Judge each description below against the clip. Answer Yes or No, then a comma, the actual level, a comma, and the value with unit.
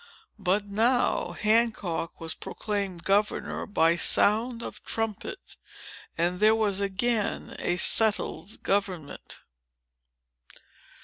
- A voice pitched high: Yes, high, 205 Hz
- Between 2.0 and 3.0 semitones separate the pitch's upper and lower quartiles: No, average, 3.4 semitones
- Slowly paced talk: Yes, slow, 90 wpm